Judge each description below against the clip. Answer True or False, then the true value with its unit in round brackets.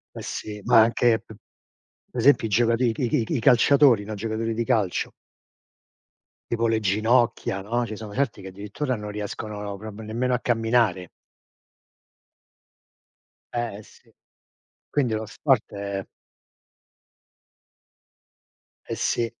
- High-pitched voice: False (110 Hz)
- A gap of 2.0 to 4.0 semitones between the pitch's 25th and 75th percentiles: True (2.4 semitones)